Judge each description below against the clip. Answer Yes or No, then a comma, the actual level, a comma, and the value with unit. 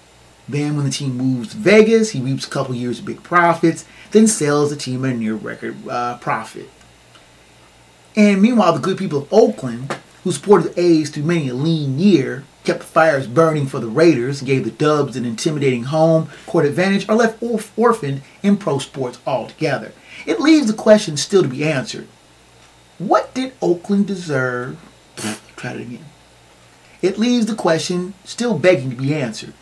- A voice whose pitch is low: No, medium, 160 Hz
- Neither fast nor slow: Yes, average, 180 wpm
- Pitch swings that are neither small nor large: No, wide, 7.0 semitones